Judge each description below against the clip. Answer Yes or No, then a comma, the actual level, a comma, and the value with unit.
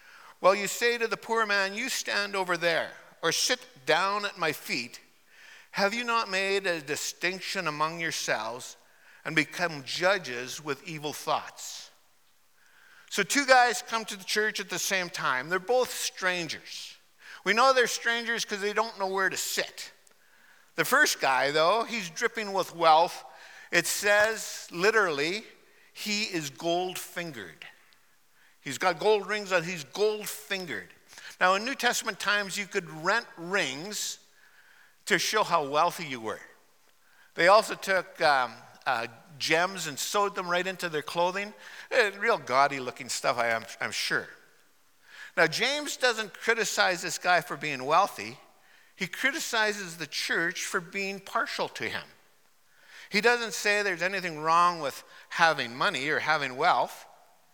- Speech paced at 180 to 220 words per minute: No, average, 150 wpm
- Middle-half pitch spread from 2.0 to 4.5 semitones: Yes, average, 4.2 semitones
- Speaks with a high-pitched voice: Yes, high, 195 Hz